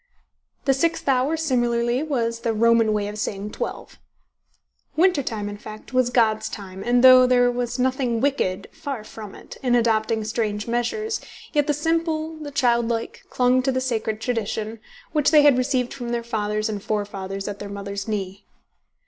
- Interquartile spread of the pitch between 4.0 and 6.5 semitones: No, average, 3.5 semitones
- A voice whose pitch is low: No, high, 235 Hz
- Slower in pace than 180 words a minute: Yes, average, 170 wpm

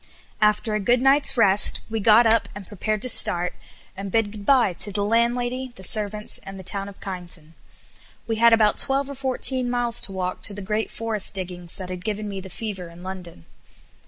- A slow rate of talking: No, average, 200 wpm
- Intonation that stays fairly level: No, average, 3.6 semitones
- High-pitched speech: Yes, high, 210 Hz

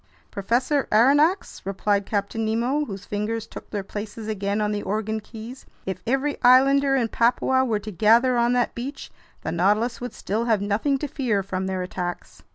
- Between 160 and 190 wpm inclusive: Yes, average, 175 wpm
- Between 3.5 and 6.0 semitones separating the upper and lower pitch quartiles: Yes, average, 3.8 semitones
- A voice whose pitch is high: Yes, high, 220 Hz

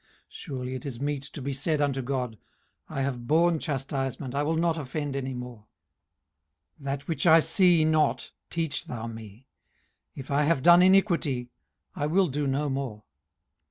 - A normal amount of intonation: Yes, average, 3.4 semitones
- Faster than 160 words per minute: Yes, average, 170 wpm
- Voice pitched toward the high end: No, medium, 140 Hz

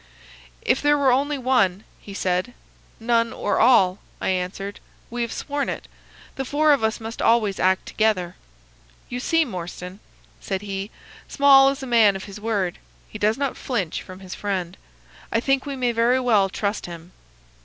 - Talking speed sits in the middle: Yes, average, 175 wpm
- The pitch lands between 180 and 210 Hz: No, high, 220 Hz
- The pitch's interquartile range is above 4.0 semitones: Yes, average, 5.1 semitones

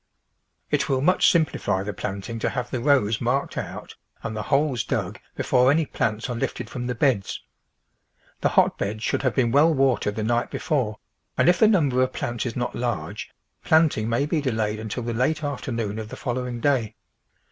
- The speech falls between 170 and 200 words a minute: Yes, average, 190 wpm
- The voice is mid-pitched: No, low, 125 Hz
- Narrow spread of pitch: No, average, 4.1 semitones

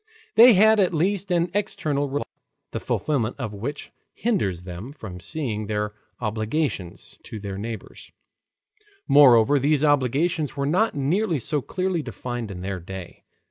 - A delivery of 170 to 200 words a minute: No, average, 145 wpm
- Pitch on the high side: No, medium, 140 Hz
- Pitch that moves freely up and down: Yes, wide, 7.7 semitones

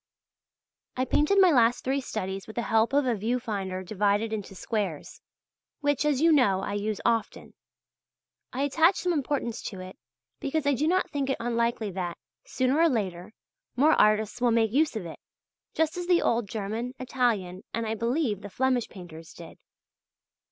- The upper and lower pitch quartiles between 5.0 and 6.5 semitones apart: Yes, average, 5.3 semitones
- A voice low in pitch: No, high, 235 Hz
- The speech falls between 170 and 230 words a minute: Yes, average, 175 wpm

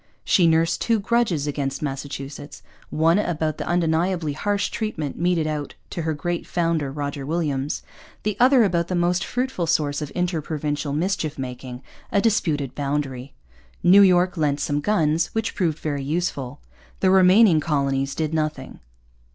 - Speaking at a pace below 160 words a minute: Yes, average, 150 wpm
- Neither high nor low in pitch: Yes, medium, 160 Hz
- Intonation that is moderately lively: Yes, average, 3.7 semitones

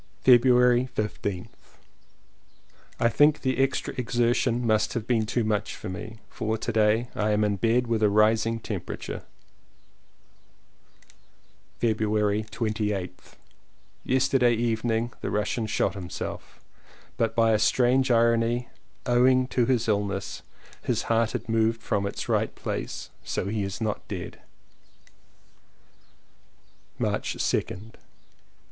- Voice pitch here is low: Yes, low, 115 Hz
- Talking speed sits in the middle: No, slow, 115 wpm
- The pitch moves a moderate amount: No, narrow, 2.2 semitones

